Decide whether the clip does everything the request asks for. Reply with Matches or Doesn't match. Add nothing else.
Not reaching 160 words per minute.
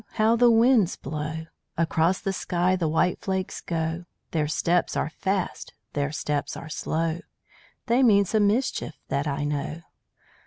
Matches